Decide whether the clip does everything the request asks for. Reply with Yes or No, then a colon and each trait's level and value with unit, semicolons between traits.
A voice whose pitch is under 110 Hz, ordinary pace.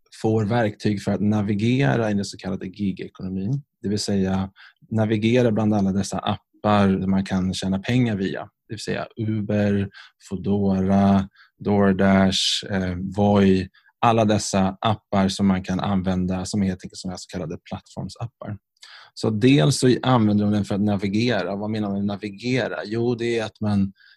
Yes: low, 100 Hz; average, 160 wpm